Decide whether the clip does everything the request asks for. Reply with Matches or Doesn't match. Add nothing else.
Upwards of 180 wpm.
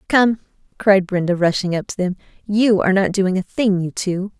Matches